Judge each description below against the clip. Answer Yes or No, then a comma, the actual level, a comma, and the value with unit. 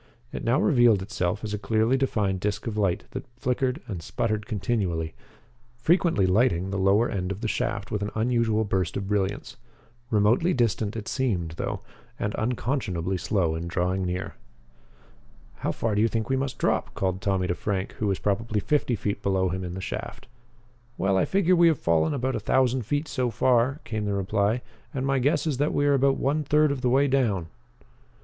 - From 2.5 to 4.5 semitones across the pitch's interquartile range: No, average, 5.1 semitones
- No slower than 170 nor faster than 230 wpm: Yes, average, 195 wpm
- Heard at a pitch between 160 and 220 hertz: No, low, 110 Hz